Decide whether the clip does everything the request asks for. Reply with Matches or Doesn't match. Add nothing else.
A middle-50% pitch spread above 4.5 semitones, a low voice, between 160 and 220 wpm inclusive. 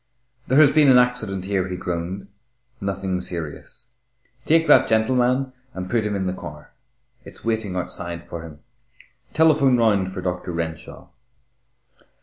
Doesn't match